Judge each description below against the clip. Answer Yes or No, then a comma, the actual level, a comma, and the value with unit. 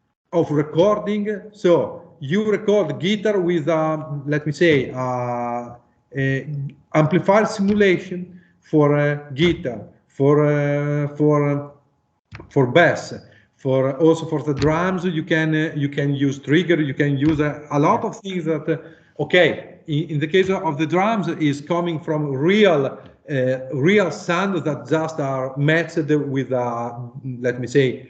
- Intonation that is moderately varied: Yes, average, 3.3 semitones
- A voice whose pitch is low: No, medium, 150 Hz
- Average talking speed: Yes, average, 145 wpm